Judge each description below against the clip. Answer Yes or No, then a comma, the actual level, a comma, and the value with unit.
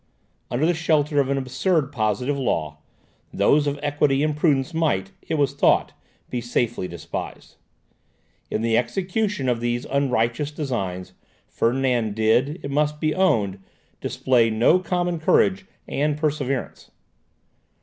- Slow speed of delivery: Yes, slow, 130 wpm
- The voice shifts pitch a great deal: No, average, 4.4 semitones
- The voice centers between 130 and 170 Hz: Yes, medium, 140 Hz